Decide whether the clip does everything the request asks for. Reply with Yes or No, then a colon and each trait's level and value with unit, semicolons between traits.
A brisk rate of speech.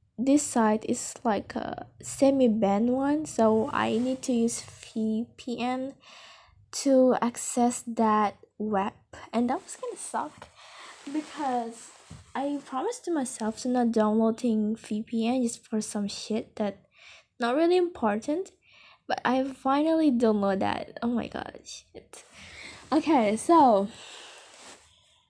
No: average, 120 wpm